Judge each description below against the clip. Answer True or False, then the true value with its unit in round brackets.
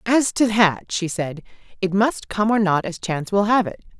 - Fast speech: True (225 wpm)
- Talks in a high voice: True (200 Hz)